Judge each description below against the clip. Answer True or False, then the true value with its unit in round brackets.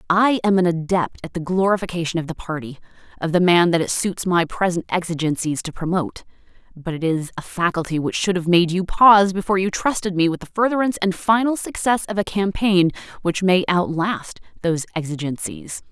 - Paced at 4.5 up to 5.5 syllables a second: False (5.7 syllables/s)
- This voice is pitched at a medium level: True (180 Hz)